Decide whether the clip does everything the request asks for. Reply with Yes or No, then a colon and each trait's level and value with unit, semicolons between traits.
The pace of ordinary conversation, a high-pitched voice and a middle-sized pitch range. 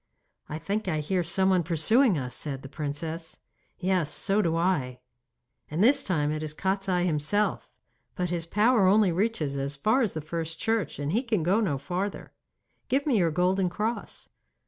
No: average, 175 wpm; medium, 180 Hz; average, 4.9 semitones